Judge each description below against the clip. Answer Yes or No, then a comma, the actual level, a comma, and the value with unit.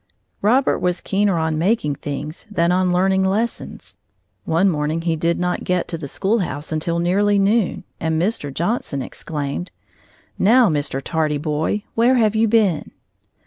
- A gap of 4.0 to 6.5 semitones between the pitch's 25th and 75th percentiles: Yes, average, 4.6 semitones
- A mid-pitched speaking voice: Yes, medium, 180 Hz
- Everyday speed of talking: Yes, average, 150 wpm